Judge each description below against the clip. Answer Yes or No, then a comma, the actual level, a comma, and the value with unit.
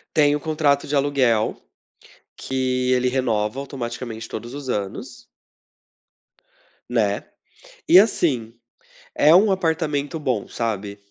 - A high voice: No, low, 130 Hz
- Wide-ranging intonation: No, average, 4.1 semitones